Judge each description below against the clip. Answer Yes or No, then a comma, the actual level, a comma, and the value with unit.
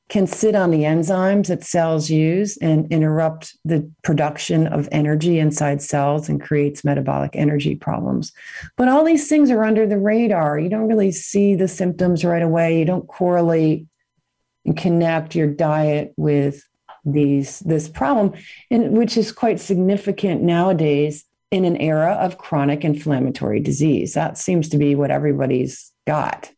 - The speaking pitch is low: No, medium, 165 Hz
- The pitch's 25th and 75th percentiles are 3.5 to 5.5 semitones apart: Yes, average, 4.2 semitones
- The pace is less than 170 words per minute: Yes, average, 155 wpm